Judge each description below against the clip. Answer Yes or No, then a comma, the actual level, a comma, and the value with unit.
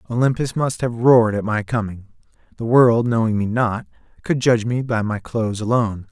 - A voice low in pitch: Yes, low, 115 Hz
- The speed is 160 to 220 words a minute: Yes, average, 185 wpm